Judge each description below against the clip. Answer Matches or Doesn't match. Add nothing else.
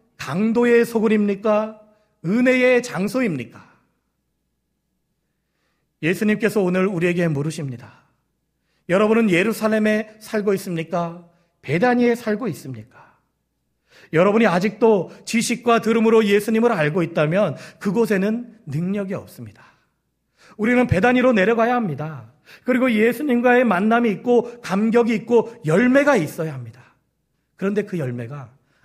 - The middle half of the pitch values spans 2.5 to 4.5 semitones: Doesn't match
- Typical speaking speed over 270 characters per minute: Matches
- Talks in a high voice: Matches